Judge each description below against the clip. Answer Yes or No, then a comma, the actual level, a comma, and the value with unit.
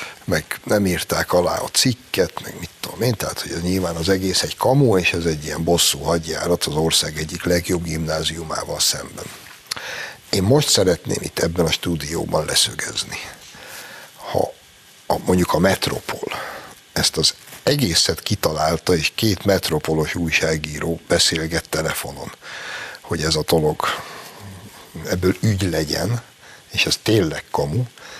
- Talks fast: No, average, 135 wpm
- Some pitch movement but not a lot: Yes, average, 3.0 semitones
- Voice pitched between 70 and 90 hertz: Yes, very low, 85 Hz